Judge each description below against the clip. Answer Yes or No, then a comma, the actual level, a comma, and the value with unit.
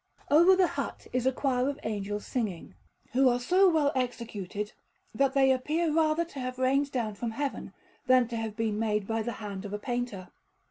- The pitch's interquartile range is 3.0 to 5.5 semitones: Yes, average, 4.4 semitones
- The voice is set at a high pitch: Yes, very high, 250 Hz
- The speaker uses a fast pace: No, average, 195 wpm